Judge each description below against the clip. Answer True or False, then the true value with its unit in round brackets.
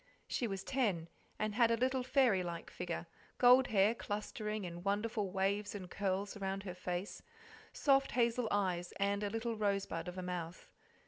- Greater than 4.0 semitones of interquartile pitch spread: False (3.5 semitones)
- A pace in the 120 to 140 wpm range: False (170 wpm)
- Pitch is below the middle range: False (205 Hz)